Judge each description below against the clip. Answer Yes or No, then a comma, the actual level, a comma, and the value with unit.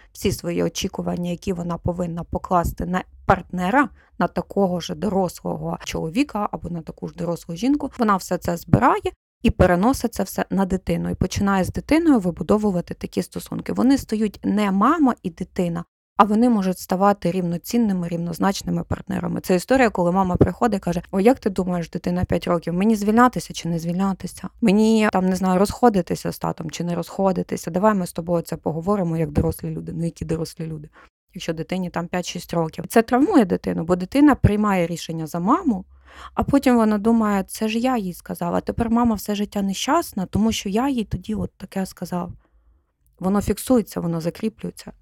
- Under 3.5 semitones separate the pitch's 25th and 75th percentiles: No, average, 4.0 semitones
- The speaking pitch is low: No, medium, 185 Hz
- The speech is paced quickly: Yes, fast, 175 wpm